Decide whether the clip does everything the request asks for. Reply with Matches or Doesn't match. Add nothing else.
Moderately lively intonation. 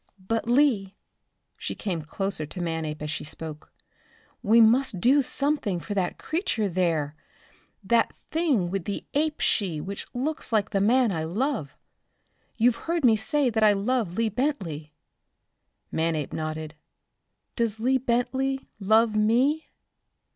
Doesn't match